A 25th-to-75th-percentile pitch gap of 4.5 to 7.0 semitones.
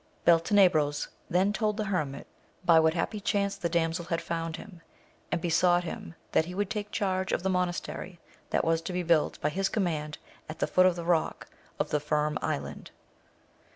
No: average, 2.7 semitones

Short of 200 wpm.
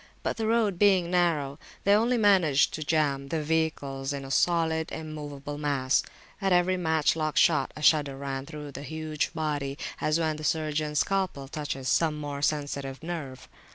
Yes: average, 170 wpm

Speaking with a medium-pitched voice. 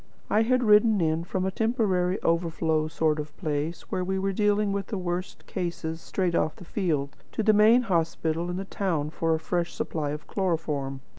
Yes: medium, 175 Hz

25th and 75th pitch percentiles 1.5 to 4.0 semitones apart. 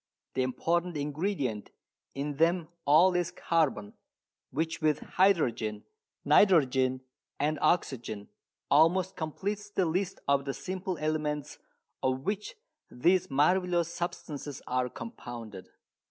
No: average, 5.2 semitones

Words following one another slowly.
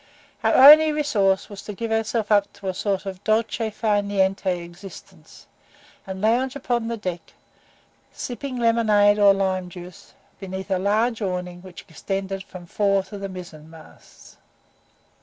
No: average, 155 wpm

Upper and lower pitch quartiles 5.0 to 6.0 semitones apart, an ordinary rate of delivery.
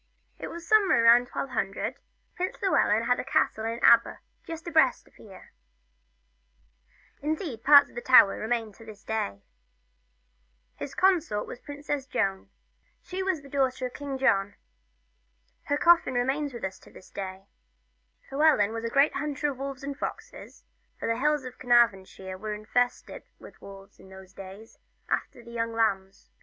Yes: wide, 5.5 semitones; average, 160 wpm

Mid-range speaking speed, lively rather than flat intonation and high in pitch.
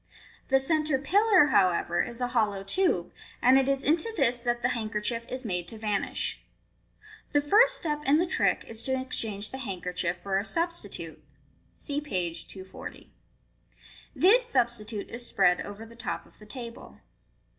Yes: average, 160 wpm; wide, 5.7 semitones; high, 240 Hz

